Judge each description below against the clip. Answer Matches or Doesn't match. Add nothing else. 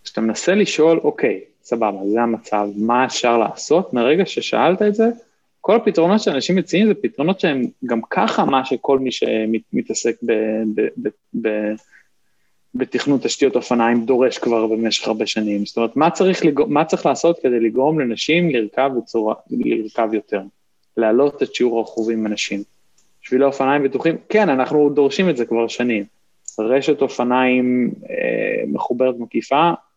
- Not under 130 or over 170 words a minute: Matches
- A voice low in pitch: Matches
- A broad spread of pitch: Matches